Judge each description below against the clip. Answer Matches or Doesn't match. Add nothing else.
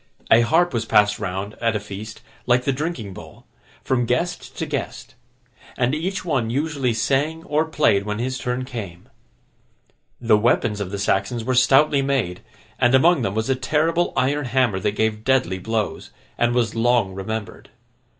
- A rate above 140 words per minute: Matches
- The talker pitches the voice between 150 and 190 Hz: Doesn't match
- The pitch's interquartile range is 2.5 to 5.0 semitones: Matches